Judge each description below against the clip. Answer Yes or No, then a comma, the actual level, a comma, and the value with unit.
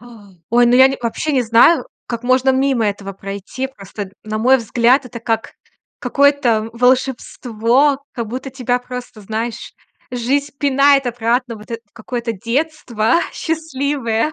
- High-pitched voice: Yes, high, 245 Hz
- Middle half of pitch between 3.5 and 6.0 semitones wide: No, average, 3.0 semitones